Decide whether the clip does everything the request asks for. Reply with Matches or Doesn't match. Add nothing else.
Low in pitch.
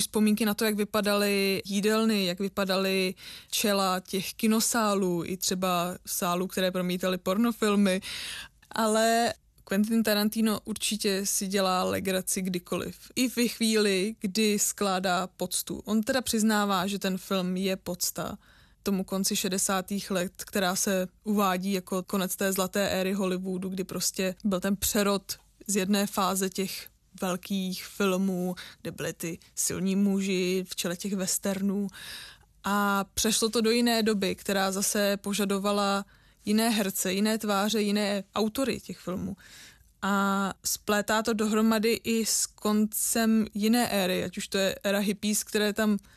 Doesn't match